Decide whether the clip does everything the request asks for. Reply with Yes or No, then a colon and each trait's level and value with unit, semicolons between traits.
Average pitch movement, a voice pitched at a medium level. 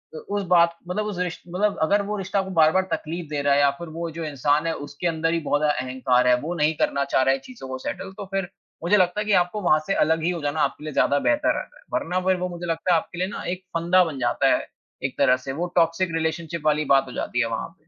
Yes: average, 3.8 semitones; medium, 165 Hz